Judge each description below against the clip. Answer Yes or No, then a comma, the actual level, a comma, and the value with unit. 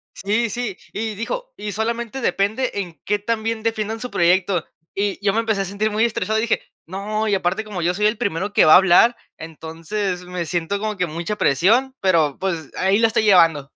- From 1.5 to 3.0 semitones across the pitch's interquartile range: No, average, 3.6 semitones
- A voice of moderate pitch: No, high, 205 Hz